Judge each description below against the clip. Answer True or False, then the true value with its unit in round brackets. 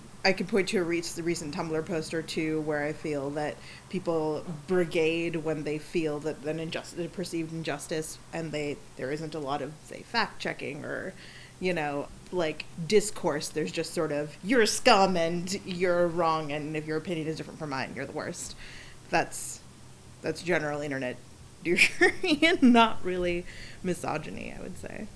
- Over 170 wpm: True (180 wpm)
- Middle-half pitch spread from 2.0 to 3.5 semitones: True (2.8 semitones)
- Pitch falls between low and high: True (165 Hz)